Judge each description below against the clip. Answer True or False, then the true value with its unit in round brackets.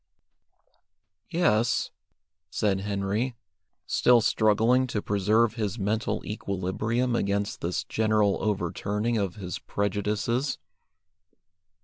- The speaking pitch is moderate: False (105 Hz)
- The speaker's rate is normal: False (85 wpm)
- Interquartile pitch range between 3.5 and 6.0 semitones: False (2.6 semitones)